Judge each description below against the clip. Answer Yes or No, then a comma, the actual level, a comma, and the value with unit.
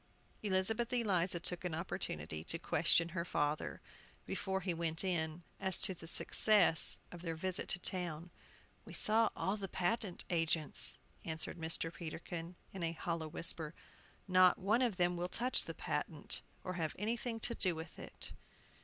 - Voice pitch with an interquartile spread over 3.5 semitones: No, average, 2.7 semitones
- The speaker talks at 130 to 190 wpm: Yes, average, 160 wpm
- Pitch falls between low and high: Yes, medium, 175 Hz